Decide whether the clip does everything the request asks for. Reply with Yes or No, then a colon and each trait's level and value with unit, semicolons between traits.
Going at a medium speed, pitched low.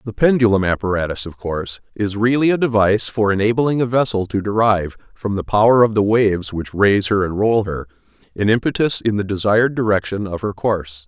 Yes: average, 195 wpm; low, 105 Hz